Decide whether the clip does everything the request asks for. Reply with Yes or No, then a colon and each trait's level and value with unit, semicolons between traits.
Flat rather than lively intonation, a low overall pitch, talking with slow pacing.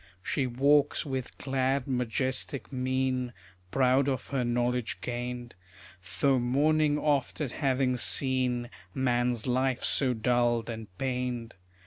Yes: narrow, 1.7 semitones; low, 130 Hz; slow, 115 wpm